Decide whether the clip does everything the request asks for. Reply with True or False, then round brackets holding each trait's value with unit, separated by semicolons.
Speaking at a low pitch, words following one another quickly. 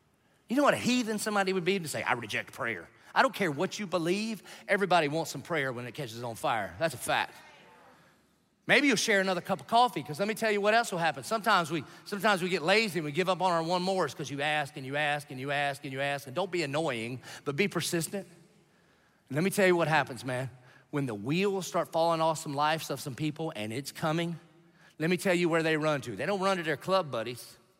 False (165 Hz; 255 wpm)